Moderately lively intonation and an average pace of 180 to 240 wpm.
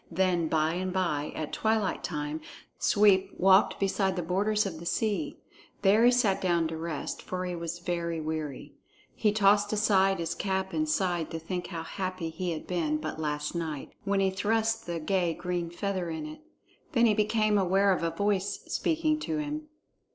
Yes: average, 3.7 semitones; average, 185 wpm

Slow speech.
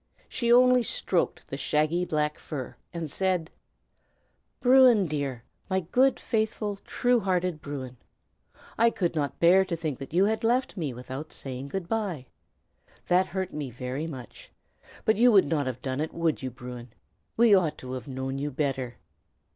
No: average, 165 wpm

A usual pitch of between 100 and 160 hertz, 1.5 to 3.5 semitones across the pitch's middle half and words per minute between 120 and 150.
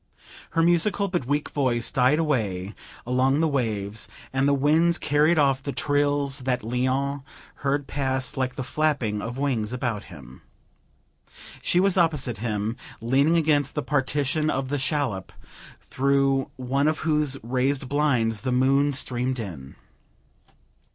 Yes: low, 135 Hz; average, 2.9 semitones; average, 140 wpm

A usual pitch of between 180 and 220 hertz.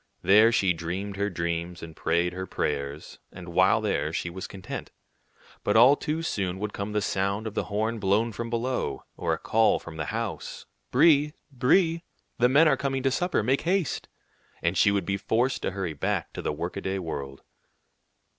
No: low, 100 Hz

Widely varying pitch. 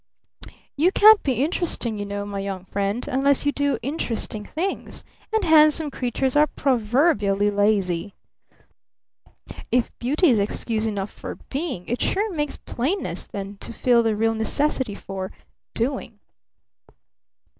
Yes: wide, 6.2 semitones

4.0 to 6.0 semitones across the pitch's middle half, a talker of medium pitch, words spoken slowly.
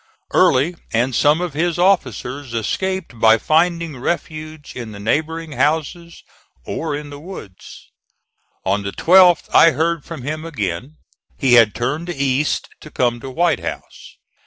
No: average, 5.3 semitones; medium, 150 Hz; average, 145 wpm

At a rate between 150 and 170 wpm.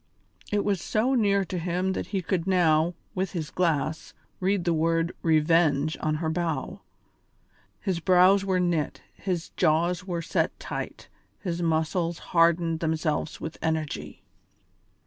No: average, 140 wpm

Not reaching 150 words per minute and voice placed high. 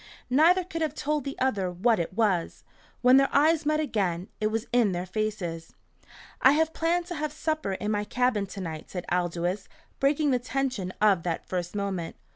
No: average, 190 wpm; high, 220 Hz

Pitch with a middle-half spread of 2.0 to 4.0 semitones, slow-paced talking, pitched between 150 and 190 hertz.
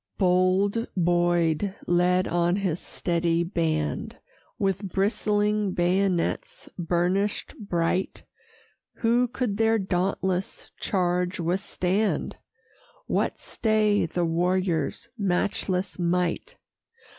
Yes: narrow, 2.6 semitones; slow, 85 wpm; medium, 185 Hz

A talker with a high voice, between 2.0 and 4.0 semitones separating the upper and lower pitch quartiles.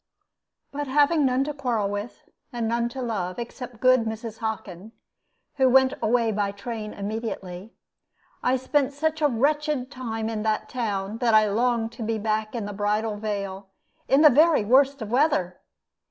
Yes: high, 230 Hz; average, 3.7 semitones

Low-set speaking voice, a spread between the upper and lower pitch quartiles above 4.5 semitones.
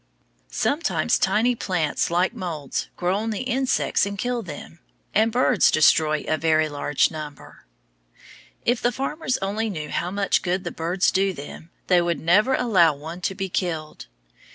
No: medium, 185 Hz; wide, 5.6 semitones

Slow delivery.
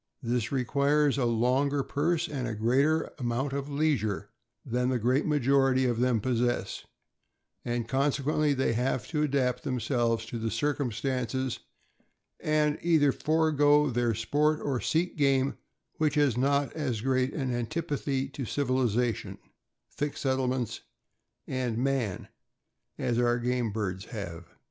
Yes: slow, 130 wpm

